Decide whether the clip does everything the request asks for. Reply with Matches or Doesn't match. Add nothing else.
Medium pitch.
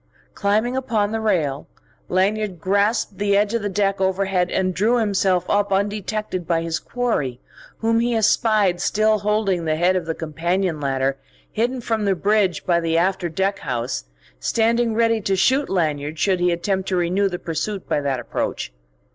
Doesn't match